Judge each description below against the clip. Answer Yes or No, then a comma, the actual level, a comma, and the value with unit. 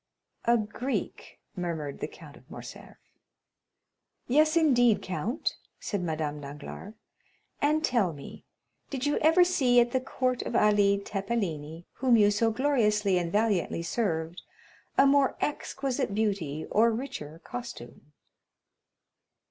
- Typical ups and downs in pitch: No, wide, 6.6 semitones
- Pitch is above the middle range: Yes, high, 215 Hz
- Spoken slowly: Yes, slow, 125 wpm